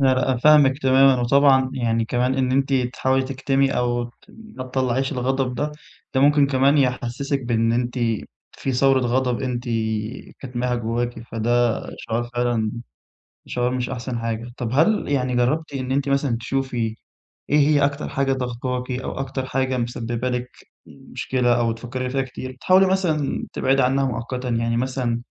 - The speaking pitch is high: No, low, 130 Hz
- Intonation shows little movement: Yes, narrow, 1.9 semitones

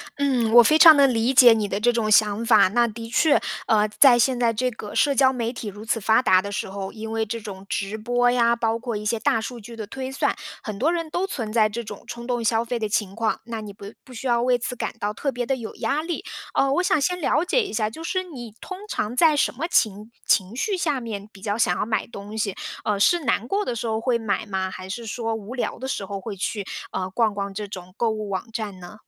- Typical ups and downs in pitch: Yes, average, 3.1 semitones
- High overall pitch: Yes, high, 230 Hz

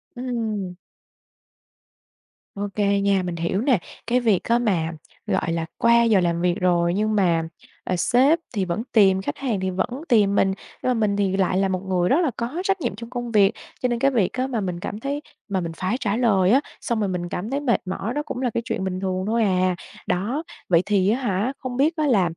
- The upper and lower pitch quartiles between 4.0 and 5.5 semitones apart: Yes, average, 4.6 semitones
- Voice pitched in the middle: No, high, 205 Hz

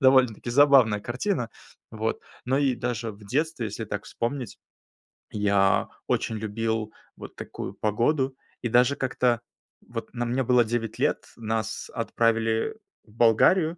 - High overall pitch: No, low, 120 Hz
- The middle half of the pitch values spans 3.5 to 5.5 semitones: No, average, 2.9 semitones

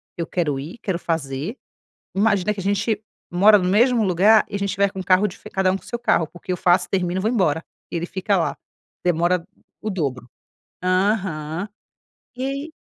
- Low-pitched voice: No, high, 190 Hz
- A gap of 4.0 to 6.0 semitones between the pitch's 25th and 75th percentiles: No, average, 3.2 semitones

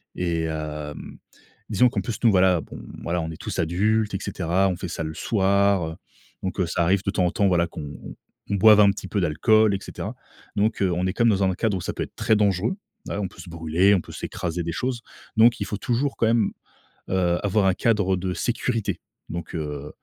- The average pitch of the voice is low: Yes, very low, 95 Hz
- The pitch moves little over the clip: No, average, 3.8 semitones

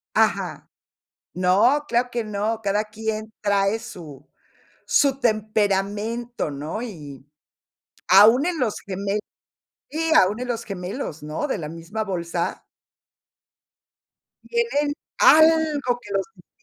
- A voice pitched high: Yes, high, 215 Hz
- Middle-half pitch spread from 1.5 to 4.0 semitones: No, average, 4.6 semitones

